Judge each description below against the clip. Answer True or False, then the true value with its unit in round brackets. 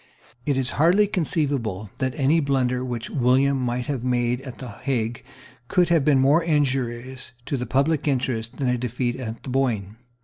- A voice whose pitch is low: True (130 Hz)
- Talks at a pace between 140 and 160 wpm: False (175 wpm)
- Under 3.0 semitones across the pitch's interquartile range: True (2.6 semitones)